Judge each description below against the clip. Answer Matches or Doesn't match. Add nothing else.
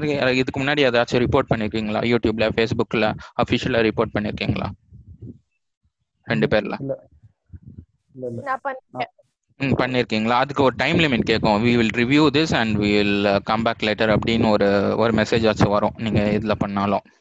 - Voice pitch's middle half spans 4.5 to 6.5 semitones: Doesn't match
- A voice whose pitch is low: Matches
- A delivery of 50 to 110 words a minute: Doesn't match